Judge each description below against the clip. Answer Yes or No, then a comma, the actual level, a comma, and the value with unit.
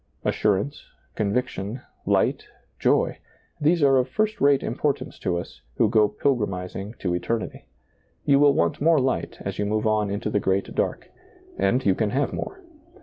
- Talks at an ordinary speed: Yes, average, 160 wpm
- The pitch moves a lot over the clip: Yes, wide, 5.7 semitones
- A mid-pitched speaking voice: No, low, 110 Hz